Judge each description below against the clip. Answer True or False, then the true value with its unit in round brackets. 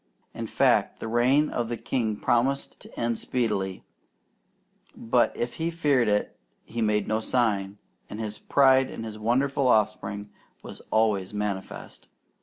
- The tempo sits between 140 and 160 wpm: True (145 wpm)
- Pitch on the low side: True (115 Hz)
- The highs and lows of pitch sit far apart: False (3.2 semitones)